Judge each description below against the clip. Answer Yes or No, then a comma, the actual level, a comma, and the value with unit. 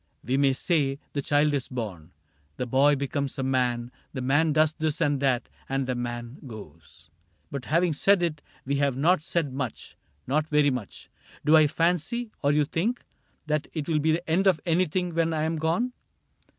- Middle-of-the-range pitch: Yes, medium, 145 Hz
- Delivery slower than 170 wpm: No, average, 190 wpm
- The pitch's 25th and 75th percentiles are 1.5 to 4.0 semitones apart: Yes, average, 3.4 semitones